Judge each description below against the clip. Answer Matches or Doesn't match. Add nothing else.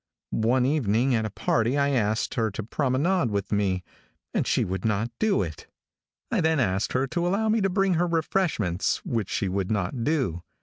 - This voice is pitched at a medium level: Doesn't match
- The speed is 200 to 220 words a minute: Doesn't match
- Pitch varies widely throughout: Matches